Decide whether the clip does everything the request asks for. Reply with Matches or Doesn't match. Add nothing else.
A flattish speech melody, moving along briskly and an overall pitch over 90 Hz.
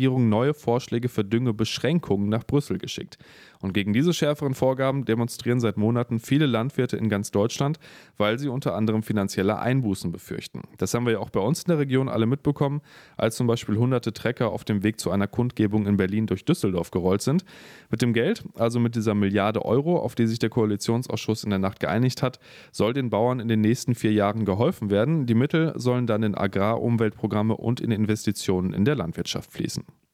Doesn't match